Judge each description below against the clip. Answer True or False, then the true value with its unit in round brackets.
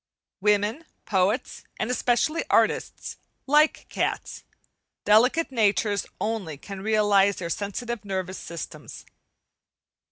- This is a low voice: False (210 Hz)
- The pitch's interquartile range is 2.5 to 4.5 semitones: True (3.4 semitones)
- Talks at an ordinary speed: False (95 wpm)